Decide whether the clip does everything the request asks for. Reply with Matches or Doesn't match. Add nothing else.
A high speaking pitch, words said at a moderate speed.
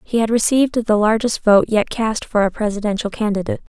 Matches